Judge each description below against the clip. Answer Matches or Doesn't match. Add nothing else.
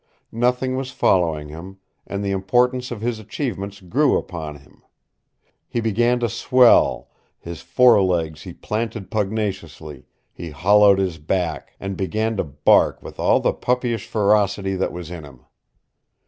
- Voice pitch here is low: Matches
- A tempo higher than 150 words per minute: Doesn't match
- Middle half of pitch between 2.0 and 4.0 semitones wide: Doesn't match